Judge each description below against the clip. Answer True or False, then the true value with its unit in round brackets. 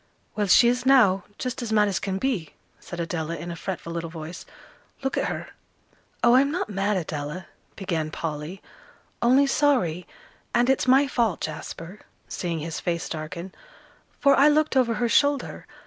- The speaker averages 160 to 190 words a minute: True (165 wpm)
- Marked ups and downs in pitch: True (7.2 semitones)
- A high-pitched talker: True (195 Hz)